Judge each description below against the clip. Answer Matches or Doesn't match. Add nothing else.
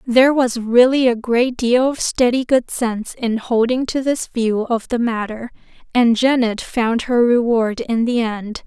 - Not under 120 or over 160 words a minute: Doesn't match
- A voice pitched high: Matches